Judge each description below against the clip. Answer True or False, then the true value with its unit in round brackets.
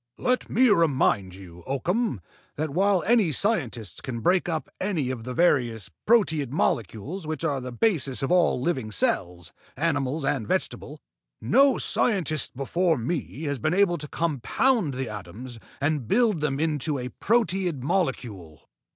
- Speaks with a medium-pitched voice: True (150 Hz)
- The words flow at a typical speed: True (150 wpm)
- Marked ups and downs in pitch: True (6.1 semitones)